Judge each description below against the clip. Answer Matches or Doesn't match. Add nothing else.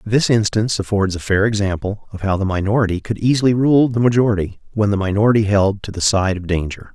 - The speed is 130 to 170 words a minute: Doesn't match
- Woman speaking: Doesn't match